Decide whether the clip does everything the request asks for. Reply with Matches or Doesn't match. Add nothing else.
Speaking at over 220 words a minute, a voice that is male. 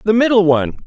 Doesn't match